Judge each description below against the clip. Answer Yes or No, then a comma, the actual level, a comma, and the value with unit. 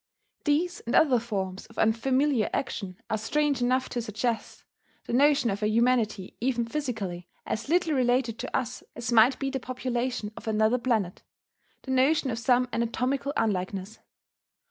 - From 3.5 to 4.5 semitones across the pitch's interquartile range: No, average, 3.1 semitones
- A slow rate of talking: No, average, 155 wpm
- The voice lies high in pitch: Yes, high, 240 Hz